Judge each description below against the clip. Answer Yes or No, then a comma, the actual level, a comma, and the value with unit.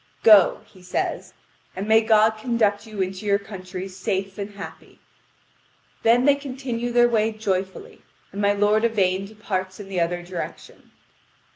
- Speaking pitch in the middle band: No, high, 205 Hz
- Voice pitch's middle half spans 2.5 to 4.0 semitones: Yes, average, 2.8 semitones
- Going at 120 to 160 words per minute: Yes, average, 150 wpm